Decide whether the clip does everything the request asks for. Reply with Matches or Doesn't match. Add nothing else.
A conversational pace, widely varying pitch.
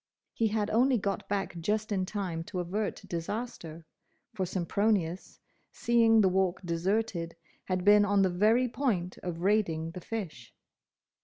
Doesn't match